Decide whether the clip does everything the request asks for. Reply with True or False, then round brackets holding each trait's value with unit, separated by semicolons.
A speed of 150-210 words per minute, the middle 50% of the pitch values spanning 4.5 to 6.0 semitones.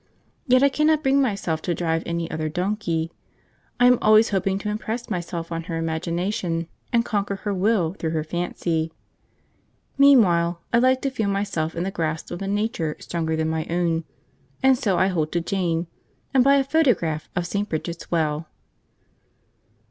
True (170 wpm; 4.9 semitones)